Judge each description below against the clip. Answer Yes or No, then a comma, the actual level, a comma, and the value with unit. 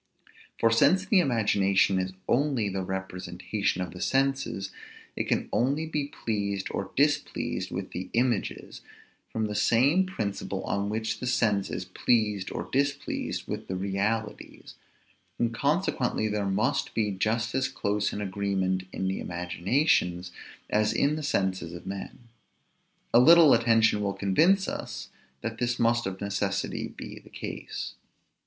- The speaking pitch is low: Yes, low, 105 Hz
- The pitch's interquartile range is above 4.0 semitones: Yes, average, 4.5 semitones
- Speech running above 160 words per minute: No, average, 145 wpm